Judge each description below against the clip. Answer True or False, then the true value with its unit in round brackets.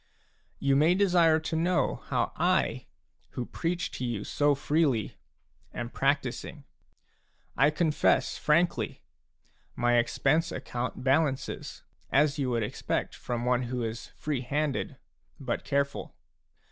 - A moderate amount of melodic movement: True (4.1 semitones)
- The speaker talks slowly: True (120 wpm)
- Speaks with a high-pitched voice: False (140 Hz)